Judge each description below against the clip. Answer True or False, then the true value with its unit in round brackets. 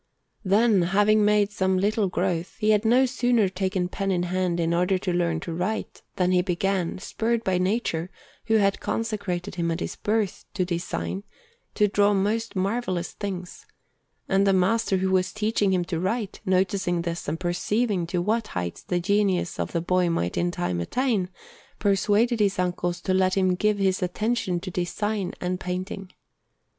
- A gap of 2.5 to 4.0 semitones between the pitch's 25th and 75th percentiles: True (2.8 semitones)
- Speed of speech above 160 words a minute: True (175 wpm)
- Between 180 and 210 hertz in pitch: True (190 Hz)